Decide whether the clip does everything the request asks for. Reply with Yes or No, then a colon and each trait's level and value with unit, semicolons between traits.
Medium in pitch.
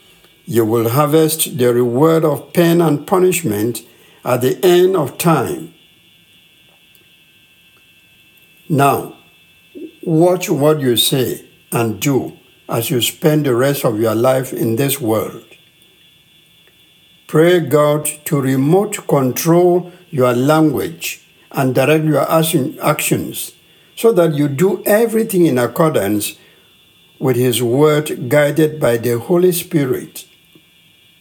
Yes: medium, 155 Hz